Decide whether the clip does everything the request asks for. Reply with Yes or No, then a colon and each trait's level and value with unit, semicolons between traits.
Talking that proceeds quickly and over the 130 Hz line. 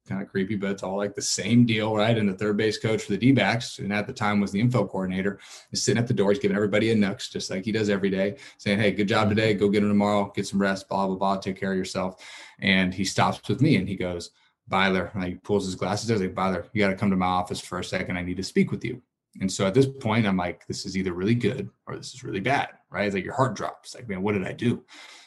No: fast, 295 wpm; low, 100 Hz